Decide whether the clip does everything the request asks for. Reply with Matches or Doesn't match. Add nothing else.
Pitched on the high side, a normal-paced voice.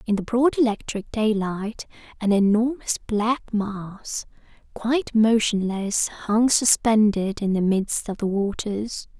Doesn't match